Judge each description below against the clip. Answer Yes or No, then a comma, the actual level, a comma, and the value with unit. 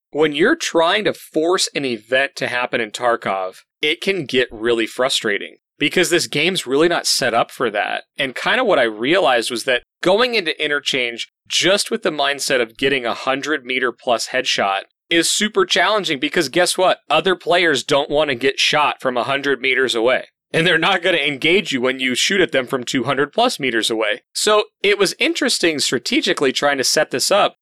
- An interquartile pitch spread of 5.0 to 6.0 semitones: Yes, wide, 5.4 semitones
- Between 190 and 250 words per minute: Yes, average, 200 wpm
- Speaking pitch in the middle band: Yes, medium, 145 Hz